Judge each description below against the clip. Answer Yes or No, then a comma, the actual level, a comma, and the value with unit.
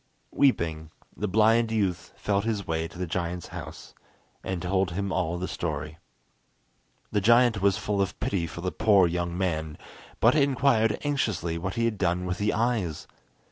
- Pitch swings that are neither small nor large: Yes, average, 4.3 semitones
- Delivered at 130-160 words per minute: No, average, 170 wpm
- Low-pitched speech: Yes, very low, 95 Hz